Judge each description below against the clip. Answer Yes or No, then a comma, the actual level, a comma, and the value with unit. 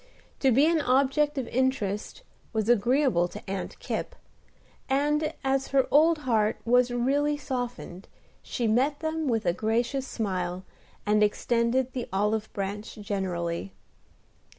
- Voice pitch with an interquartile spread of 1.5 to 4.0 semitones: No, average, 4.7 semitones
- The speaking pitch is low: No, high, 240 Hz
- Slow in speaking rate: Yes, slow, 130 wpm